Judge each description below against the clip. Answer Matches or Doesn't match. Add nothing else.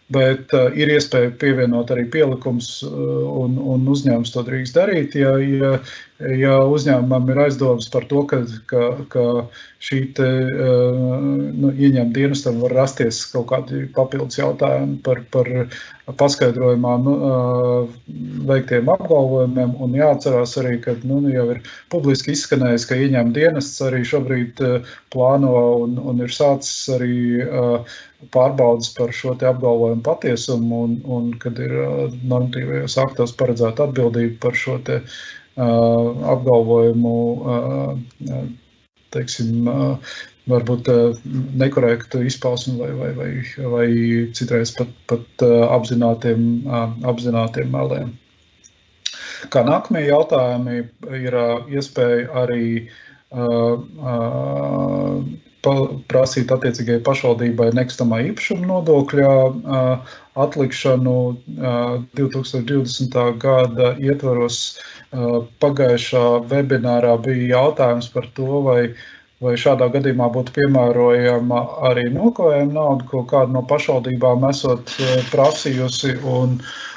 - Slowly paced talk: Matches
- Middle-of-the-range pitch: Doesn't match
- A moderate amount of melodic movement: Doesn't match